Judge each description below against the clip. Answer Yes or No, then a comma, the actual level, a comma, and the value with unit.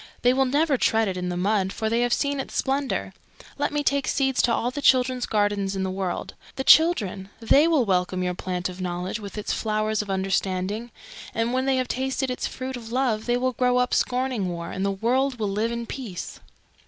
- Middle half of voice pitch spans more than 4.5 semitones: Yes, average, 5.0 semitones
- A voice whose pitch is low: No, high, 230 Hz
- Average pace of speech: No, fast, 220 wpm